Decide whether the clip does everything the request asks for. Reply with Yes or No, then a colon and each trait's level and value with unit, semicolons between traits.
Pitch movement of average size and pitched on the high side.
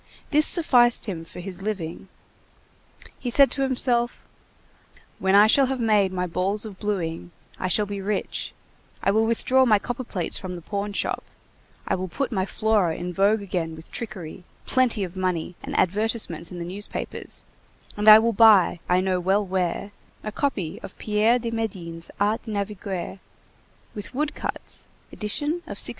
Yes: average, 3.6 semitones; high, 205 Hz